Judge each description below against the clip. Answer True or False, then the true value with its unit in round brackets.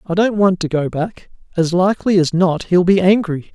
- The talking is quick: True (220 wpm)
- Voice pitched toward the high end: False (180 Hz)